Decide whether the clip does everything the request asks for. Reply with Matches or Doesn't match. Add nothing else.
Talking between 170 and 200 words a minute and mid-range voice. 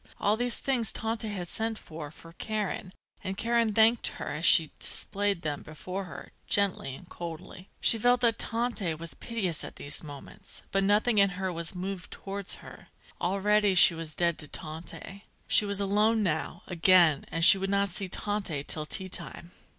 Doesn't match